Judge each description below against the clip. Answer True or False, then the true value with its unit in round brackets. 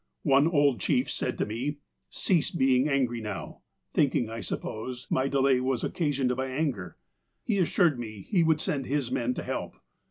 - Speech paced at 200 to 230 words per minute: False (180 wpm)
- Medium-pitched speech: False (130 Hz)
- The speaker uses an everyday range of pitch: True (3.4 semitones)